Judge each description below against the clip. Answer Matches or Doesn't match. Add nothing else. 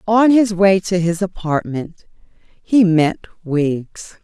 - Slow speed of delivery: Matches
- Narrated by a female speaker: Matches